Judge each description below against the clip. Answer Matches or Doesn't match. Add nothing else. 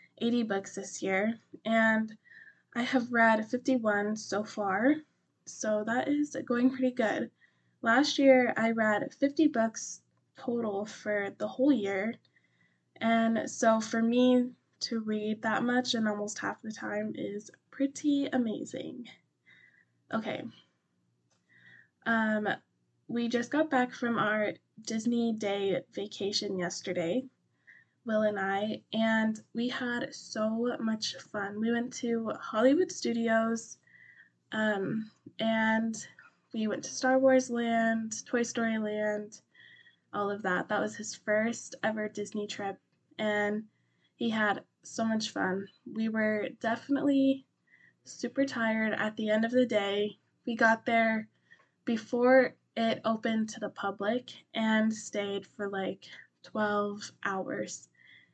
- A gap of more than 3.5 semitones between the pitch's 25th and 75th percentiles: Doesn't match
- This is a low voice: Doesn't match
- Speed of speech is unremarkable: Doesn't match